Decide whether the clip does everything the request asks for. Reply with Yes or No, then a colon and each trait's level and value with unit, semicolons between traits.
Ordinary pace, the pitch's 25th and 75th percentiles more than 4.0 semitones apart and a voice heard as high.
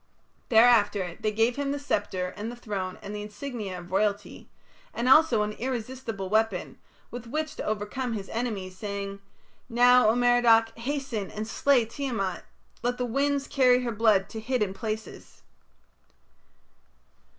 No: average, 145 wpm; average, 3.3 semitones; high, 225 Hz